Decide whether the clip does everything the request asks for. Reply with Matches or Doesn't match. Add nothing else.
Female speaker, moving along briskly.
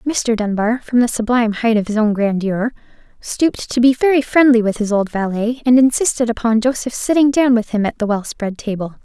Matches